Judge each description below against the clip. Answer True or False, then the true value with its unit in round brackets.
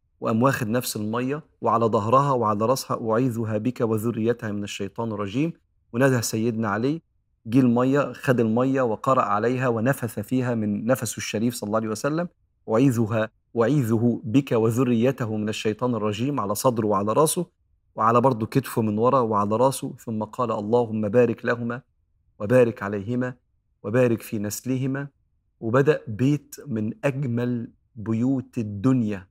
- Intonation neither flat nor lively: True (3.1 semitones)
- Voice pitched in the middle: False (115 Hz)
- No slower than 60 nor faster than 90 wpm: False (135 wpm)